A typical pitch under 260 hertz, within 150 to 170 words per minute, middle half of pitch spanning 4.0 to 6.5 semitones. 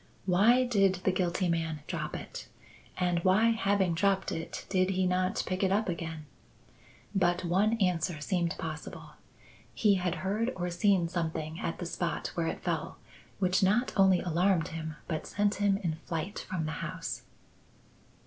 No: medium, 185 Hz; average, 160 wpm; average, 2.7 semitones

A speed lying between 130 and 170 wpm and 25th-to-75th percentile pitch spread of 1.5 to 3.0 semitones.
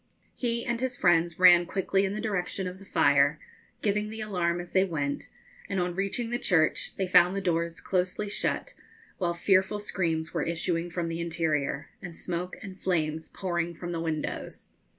No: average, 180 wpm; average, 2.7 semitones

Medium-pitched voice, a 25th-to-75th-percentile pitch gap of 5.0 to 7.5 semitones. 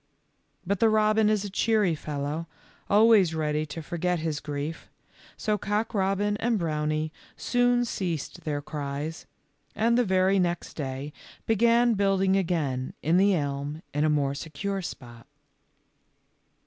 Yes: medium, 175 Hz; wide, 5.5 semitones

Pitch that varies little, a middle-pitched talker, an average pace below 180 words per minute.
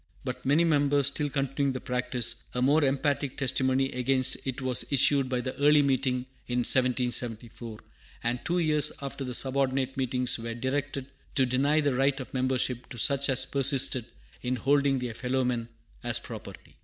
No: narrow, 1.9 semitones; low, 130 Hz; average, 170 wpm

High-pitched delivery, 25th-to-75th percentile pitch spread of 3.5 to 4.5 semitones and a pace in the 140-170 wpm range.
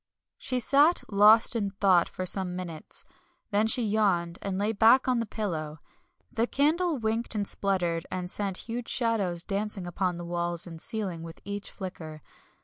Yes: high, 200 Hz; average, 4.2 semitones; average, 165 wpm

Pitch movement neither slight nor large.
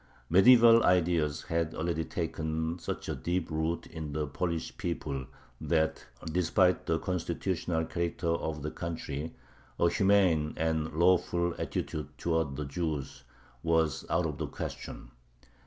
No: narrow, 1.9 semitones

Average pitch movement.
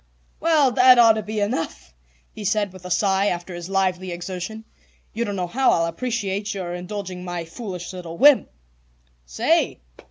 Yes: average, 3.7 semitones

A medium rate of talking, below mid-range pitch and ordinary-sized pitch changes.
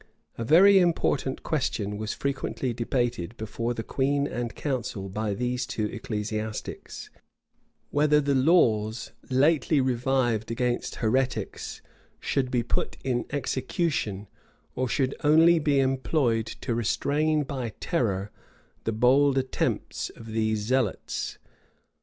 No: slow, 115 wpm; low, 125 Hz; average, 3.9 semitones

